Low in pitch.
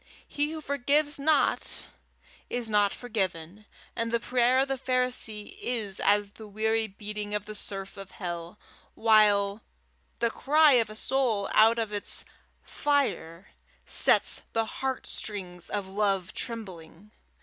No: high, 215 Hz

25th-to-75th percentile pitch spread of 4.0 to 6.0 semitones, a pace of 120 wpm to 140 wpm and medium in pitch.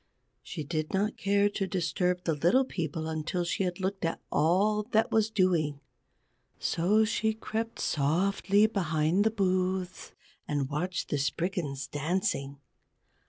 Yes: average, 4.3 semitones; slow, 135 wpm; medium, 180 Hz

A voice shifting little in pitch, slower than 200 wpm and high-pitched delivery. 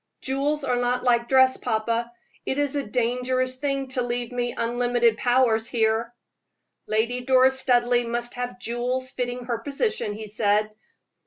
Yes: narrow, 1.7 semitones; average, 150 wpm; high, 245 Hz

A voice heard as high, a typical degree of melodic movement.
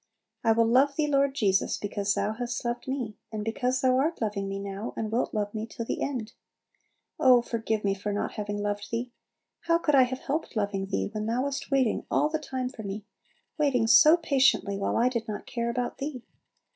Yes: high, 235 Hz; average, 4.0 semitones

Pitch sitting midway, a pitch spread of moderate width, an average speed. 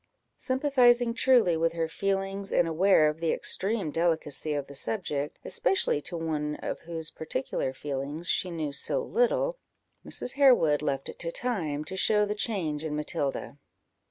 No: medium, 165 Hz; wide, 6.0 semitones; average, 155 wpm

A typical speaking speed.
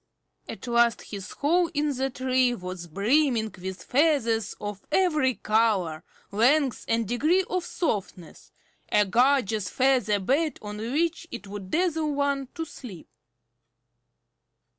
No: slow, 125 wpm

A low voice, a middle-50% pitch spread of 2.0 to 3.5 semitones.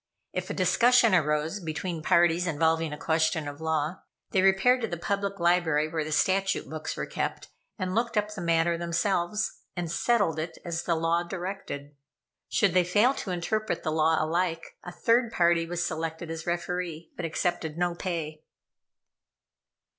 No: medium, 170 Hz; narrow, 2.6 semitones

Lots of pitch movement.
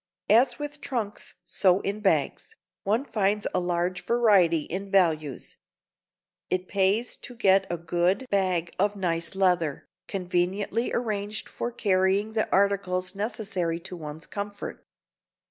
No: average, 2.8 semitones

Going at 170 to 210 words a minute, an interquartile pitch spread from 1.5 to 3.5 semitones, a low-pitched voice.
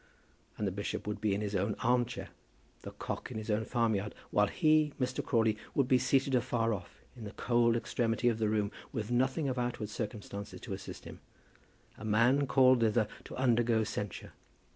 Yes: average, 190 wpm; average, 3.0 semitones; low, 115 Hz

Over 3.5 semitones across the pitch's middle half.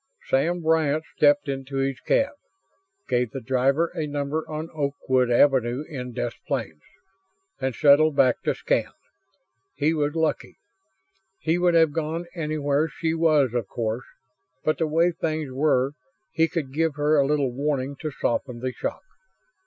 No: average, 3.2 semitones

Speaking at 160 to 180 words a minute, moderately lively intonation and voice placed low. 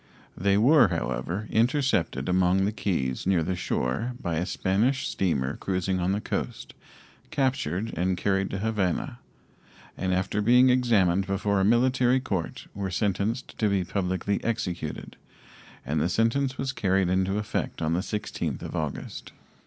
No: average, 150 wpm; average, 3.8 semitones; very low, 95 Hz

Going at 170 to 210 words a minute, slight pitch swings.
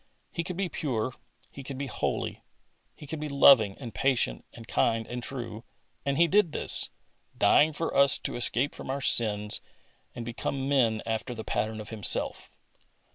No: average, 175 wpm; average, 3.9 semitones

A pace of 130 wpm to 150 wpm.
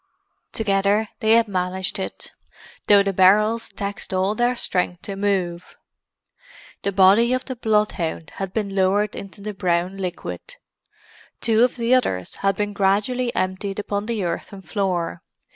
Yes: average, 145 wpm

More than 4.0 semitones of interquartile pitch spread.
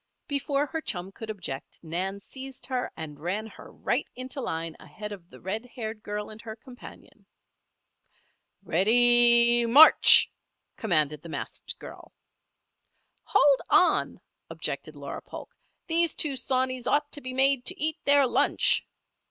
Yes: wide, 5.5 semitones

